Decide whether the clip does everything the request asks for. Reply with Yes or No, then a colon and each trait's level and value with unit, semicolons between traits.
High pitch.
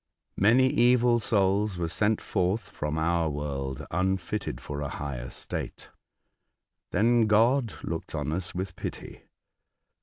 No: very low, 95 Hz